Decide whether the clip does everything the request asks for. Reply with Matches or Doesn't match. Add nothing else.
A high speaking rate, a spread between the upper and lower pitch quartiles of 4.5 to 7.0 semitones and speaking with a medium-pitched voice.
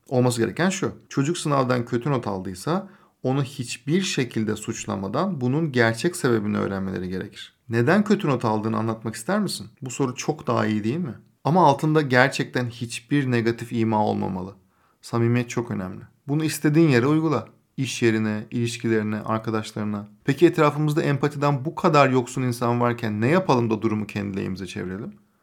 Doesn't match